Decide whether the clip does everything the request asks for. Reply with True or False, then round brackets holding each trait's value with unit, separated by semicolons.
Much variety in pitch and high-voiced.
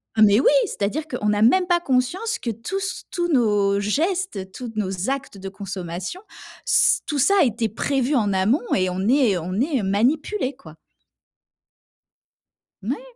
True (6.8 semitones; 235 Hz)